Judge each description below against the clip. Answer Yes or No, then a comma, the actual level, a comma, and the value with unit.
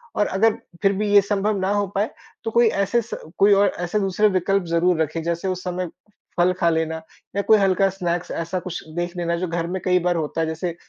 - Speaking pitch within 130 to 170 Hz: No, medium, 185 Hz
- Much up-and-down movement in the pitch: No, average, 2.8 semitones